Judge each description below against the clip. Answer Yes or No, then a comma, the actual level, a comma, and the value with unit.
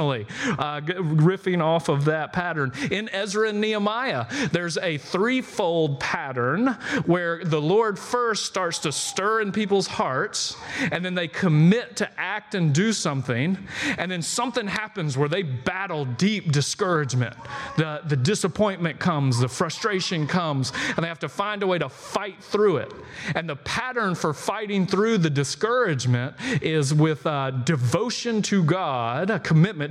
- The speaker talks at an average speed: Yes, average, 155 wpm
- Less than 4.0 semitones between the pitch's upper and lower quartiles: No, average, 5.2 semitones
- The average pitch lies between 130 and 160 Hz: No, medium, 175 Hz